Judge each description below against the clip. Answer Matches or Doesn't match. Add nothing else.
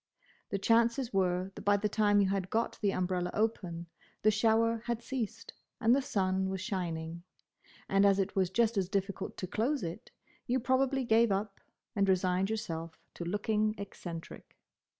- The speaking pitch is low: Doesn't match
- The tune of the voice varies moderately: Matches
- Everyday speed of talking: Matches